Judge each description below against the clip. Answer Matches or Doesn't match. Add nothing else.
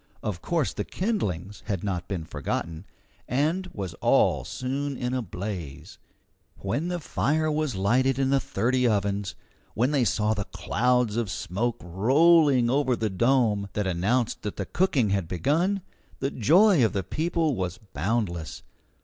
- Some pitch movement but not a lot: Doesn't match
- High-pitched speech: Doesn't match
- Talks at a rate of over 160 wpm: Doesn't match